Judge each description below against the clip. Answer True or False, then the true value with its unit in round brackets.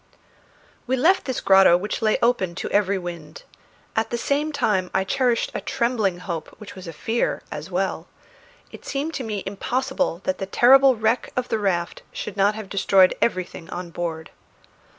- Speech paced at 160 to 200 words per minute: True (175 wpm)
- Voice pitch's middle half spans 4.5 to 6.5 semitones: True (4.9 semitones)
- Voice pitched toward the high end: True (200 Hz)